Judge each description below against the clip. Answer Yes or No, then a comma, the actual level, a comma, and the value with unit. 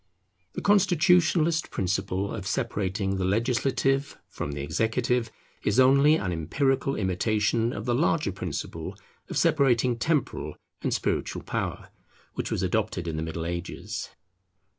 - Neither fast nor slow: No, slow, 130 wpm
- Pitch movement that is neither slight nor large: No, wide, 6.5 semitones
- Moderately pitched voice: No, low, 115 Hz